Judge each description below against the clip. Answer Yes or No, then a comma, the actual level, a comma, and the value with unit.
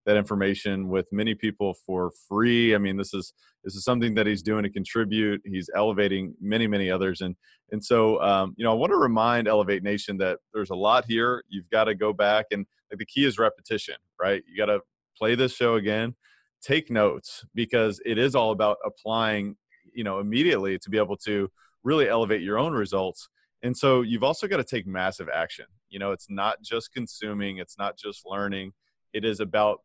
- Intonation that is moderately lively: No, narrow, 2.3 semitones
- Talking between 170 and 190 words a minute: No, fast, 205 wpm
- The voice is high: No, low, 105 Hz